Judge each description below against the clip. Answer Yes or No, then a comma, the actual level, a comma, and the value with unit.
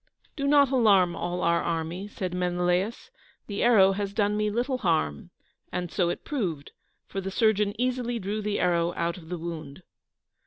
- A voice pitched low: No, high, 190 Hz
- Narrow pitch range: No, average, 3.9 semitones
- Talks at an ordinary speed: Yes, average, 170 wpm